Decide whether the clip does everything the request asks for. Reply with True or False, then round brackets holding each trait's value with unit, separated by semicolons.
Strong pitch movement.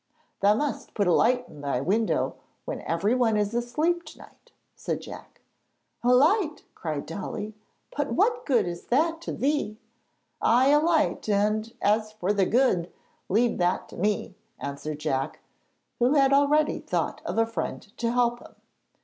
True (5.9 semitones)